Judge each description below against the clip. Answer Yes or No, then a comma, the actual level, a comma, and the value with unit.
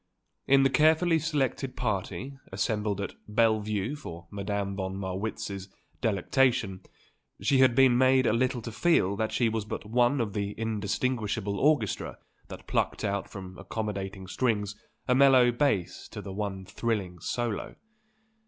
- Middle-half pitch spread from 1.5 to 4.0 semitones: No, average, 4.5 semitones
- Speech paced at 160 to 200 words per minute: No, average, 145 wpm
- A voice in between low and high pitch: No, low, 110 Hz